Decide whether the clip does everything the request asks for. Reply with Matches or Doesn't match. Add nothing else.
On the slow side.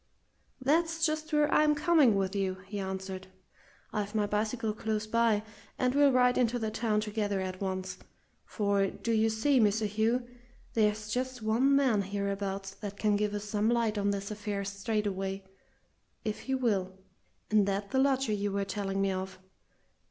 Doesn't match